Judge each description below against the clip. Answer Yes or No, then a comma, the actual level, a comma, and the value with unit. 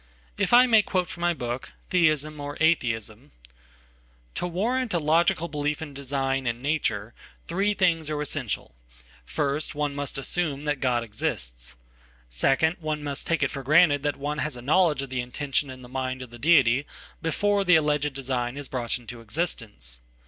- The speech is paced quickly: No, average, 175 wpm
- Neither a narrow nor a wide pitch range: Yes, average, 4.4 semitones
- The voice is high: No, medium, 145 Hz